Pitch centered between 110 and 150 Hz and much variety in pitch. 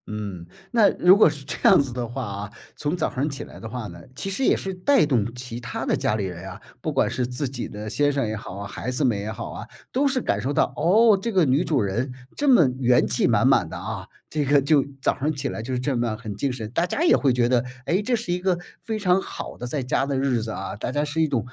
Yes: low, 135 Hz; wide, 6.1 semitones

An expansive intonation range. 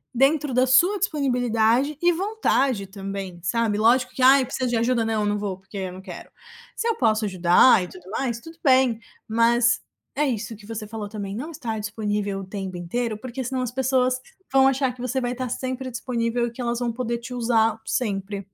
No: average, 3.6 semitones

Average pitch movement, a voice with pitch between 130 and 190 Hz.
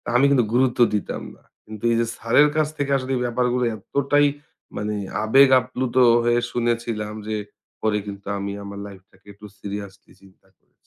No: average, 3.9 semitones; low, 115 Hz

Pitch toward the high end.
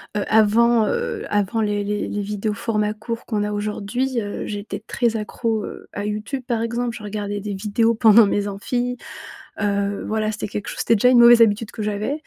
Yes: high, 215 Hz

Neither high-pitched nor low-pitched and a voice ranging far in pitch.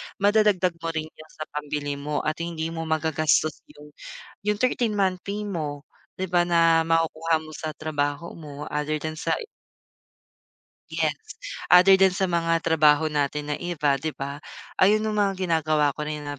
No: medium, 160 Hz; average, 2.8 semitones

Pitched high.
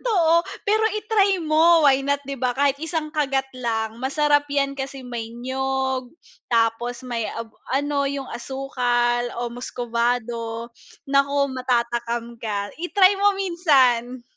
Yes: very high, 265 Hz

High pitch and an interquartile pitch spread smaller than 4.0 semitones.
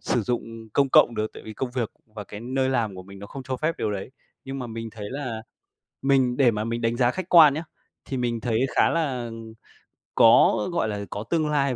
No: low, 120 Hz; average, 3.3 semitones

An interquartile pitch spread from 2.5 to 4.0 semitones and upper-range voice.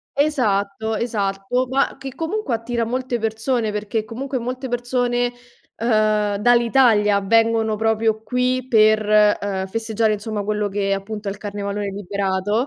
Yes: average, 2.9 semitones; high, 220 Hz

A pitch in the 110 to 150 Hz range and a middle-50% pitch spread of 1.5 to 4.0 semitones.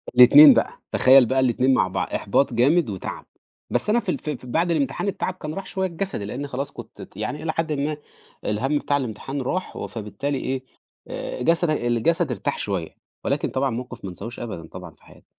No: low, 135 Hz; average, 4.6 semitones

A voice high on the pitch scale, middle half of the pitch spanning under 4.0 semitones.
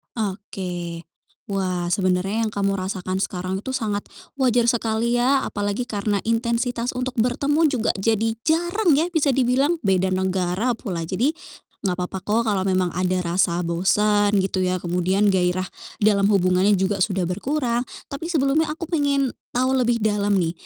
No: high, 205 Hz; average, 4.9 semitones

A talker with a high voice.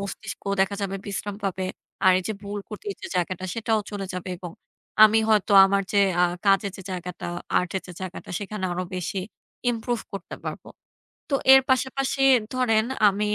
Yes: high, 200 Hz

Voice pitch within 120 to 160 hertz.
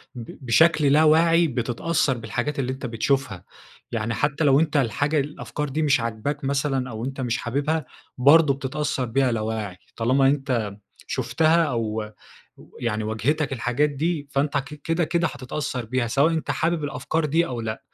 Yes: low, 135 Hz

